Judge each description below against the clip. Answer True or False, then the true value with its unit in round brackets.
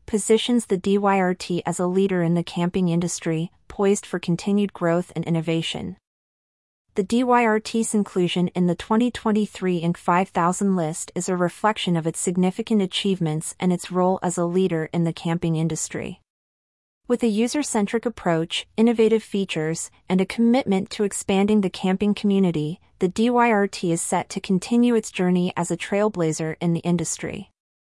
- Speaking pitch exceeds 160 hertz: True (185 Hz)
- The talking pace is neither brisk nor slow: True (150 wpm)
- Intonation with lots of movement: False (3.6 semitones)